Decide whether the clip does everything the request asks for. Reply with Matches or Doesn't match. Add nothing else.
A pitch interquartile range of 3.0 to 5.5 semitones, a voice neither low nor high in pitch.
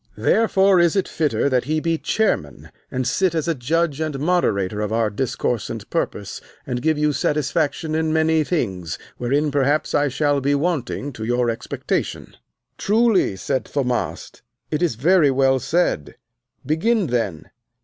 Matches